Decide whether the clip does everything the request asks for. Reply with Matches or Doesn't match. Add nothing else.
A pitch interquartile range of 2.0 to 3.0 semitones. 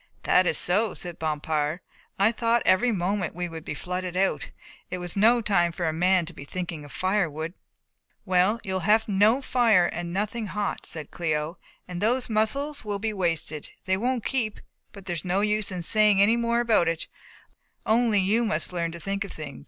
Doesn't match